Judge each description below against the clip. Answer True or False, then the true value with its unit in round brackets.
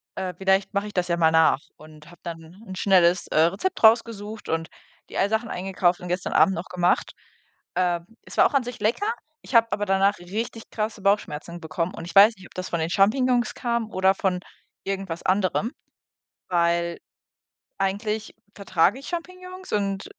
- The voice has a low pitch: False (195 Hz)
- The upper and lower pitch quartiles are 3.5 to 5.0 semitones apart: True (4.0 semitones)